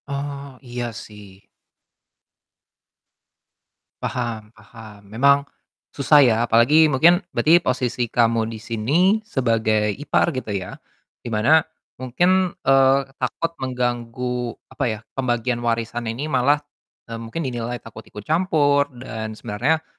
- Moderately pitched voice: No, low, 125 Hz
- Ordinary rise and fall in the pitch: Yes, average, 3.8 semitones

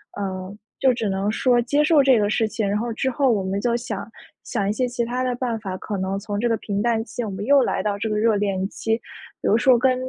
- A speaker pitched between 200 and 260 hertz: Yes, high, 225 Hz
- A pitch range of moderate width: Yes, average, 3.4 semitones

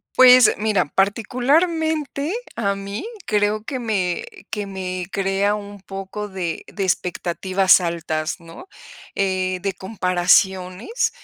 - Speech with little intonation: No, average, 3.1 semitones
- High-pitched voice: Yes, high, 195 Hz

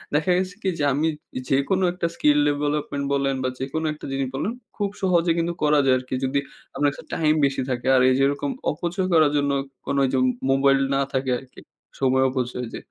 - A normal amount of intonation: Yes, average, 3.2 semitones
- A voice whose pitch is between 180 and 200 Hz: No, medium, 140 Hz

